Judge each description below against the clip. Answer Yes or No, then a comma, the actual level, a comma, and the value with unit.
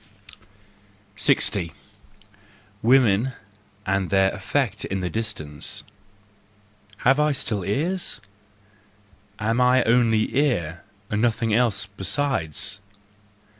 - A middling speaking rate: No, slow, 90 wpm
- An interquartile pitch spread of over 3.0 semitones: Yes, average, 4.5 semitones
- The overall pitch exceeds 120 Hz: No, low, 110 Hz